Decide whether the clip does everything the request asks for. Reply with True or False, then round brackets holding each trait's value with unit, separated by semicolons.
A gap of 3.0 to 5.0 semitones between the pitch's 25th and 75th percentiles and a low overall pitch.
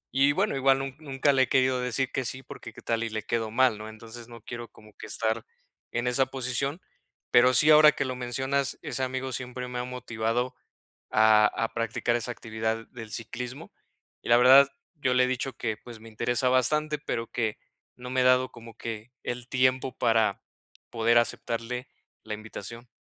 False (2.4 semitones; 125 Hz)